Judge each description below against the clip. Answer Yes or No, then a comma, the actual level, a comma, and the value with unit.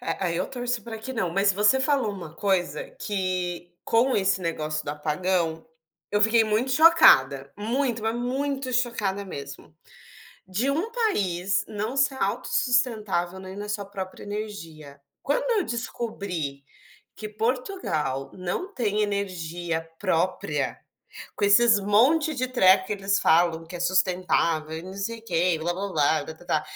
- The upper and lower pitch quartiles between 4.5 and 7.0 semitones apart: Yes, average, 5.3 semitones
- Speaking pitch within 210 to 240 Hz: No, high, 200 Hz